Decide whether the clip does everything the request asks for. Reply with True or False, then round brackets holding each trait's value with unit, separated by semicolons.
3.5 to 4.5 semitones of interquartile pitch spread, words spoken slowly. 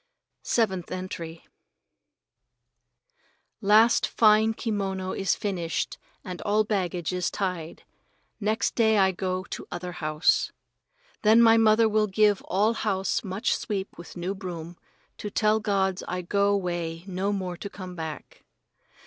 False (2.8 semitones; 130 wpm)